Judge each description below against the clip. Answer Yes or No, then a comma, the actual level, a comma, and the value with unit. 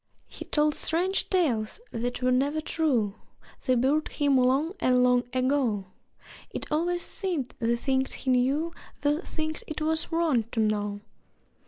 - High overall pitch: Yes, very high, 270 Hz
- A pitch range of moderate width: Yes, average, 4.1 semitones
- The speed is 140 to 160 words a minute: Yes, average, 150 wpm